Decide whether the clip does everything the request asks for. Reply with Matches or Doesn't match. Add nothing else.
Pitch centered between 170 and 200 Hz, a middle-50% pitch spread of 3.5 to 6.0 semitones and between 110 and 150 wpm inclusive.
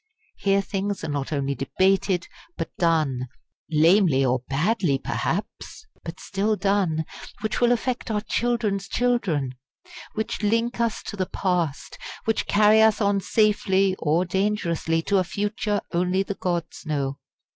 Matches